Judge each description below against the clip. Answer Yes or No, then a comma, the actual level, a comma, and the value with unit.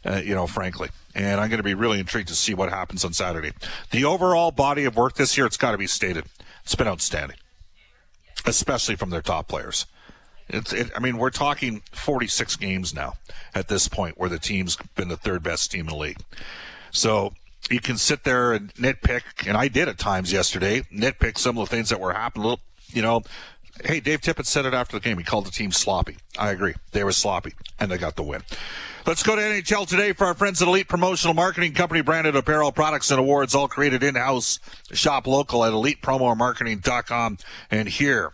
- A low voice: Yes, low, 115 Hz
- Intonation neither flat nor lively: No, wide, 6.8 semitones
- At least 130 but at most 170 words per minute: No, fast, 205 wpm